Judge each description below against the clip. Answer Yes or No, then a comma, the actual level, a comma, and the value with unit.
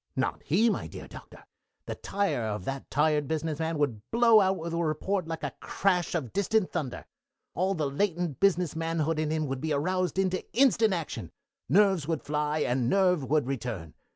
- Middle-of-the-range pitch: Yes, medium, 160 Hz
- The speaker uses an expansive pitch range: No, average, 4.2 semitones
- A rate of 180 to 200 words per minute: Yes, average, 185 wpm